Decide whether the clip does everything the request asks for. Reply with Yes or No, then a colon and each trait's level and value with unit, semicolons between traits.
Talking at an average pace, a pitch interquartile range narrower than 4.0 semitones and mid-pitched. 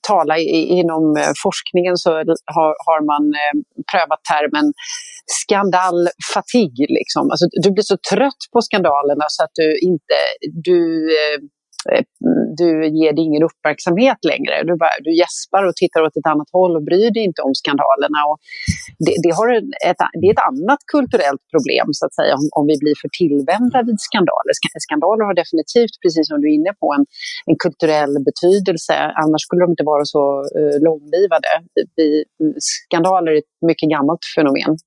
No: average, 155 wpm; wide, 5.5 semitones; medium, 170 Hz